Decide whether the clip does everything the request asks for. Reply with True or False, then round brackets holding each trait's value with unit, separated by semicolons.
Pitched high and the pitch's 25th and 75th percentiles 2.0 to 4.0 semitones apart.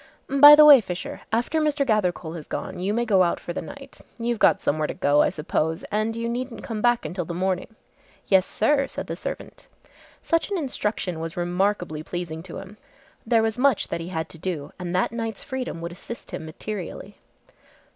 False (205 Hz; 5.5 semitones)